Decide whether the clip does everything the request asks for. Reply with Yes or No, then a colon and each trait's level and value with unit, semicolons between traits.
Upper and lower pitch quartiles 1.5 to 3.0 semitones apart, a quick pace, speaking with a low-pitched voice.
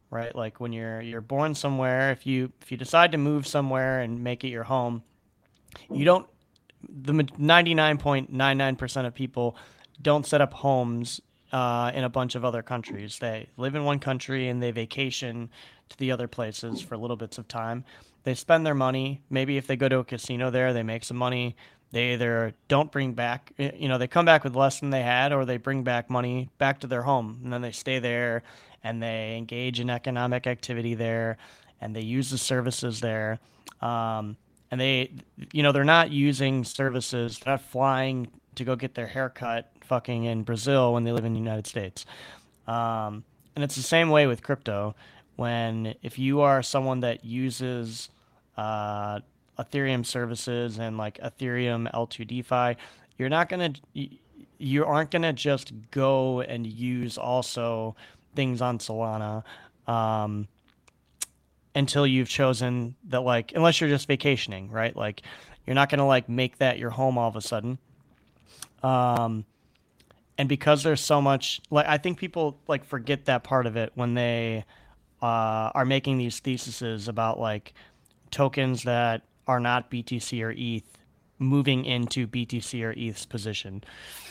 No: average, 2.7 semitones; average, 170 wpm; low, 125 Hz